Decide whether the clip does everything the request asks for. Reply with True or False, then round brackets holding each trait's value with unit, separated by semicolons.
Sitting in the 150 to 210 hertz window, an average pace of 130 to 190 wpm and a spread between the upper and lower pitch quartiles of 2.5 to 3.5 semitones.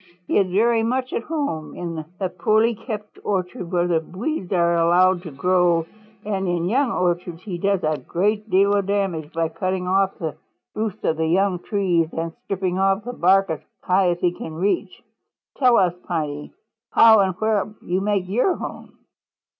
True (185 Hz; 180 wpm; 3.1 semitones)